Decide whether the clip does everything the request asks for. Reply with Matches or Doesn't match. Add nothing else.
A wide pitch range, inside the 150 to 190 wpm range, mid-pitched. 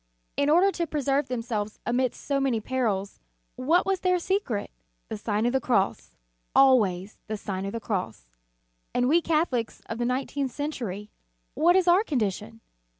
Doesn't match